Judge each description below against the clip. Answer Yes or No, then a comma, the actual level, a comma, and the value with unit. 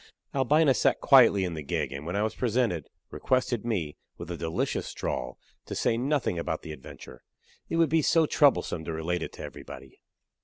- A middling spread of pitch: No, wide, 8.4 semitones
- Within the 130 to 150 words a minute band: No, average, 190 wpm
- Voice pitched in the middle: No, low, 100 Hz